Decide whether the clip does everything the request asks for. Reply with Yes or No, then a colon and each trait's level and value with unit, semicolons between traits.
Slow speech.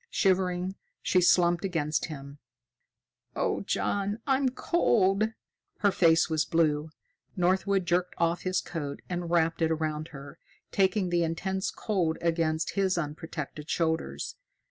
Yes: slow, 125 wpm